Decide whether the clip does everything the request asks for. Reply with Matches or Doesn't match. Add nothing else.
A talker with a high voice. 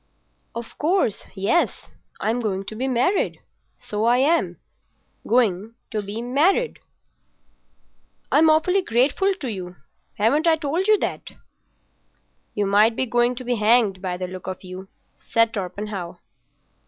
Matches